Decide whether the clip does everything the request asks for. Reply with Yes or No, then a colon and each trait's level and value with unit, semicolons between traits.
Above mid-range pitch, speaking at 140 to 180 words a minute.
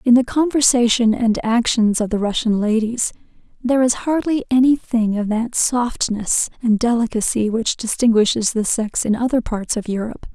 Yes: high, 230 Hz; average, 160 wpm